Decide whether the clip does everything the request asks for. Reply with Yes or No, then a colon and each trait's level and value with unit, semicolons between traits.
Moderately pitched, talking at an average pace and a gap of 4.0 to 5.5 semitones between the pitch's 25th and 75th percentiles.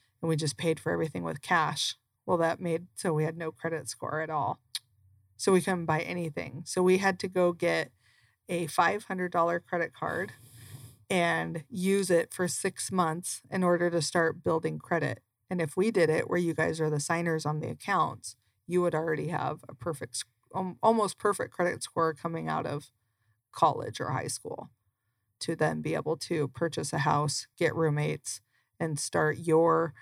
Yes: medium, 160 Hz; average, 180 wpm; average, 5.0 semitones